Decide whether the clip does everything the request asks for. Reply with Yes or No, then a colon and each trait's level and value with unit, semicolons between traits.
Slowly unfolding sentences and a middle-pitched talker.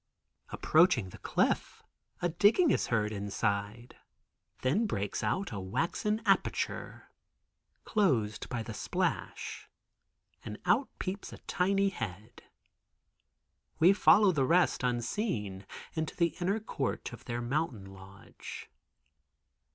No: slow, 110 wpm; low, 130 Hz